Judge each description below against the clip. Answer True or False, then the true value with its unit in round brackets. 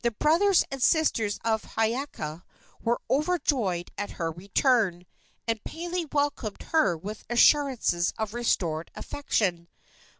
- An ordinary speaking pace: False (120 wpm)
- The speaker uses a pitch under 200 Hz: False (230 Hz)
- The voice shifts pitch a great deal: True (7.7 semitones)